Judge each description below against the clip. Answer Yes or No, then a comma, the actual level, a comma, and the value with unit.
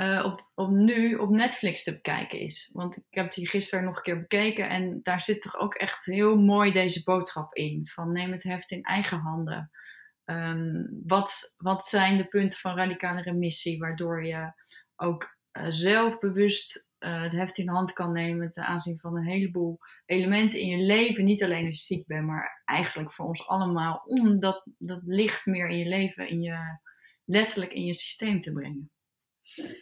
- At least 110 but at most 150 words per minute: No, average, 190 wpm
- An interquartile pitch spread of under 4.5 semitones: Yes, average, 2.7 semitones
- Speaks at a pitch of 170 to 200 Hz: Yes, medium, 185 Hz